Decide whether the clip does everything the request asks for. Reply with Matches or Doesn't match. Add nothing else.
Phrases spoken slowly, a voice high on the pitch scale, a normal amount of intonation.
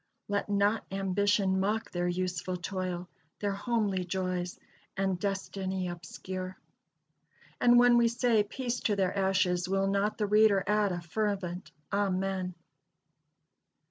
Doesn't match